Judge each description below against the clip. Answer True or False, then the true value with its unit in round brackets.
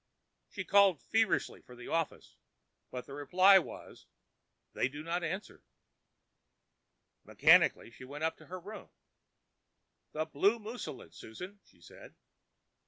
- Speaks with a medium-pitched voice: True (170 Hz)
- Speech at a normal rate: False (125 wpm)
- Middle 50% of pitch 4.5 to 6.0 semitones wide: True (5.4 semitones)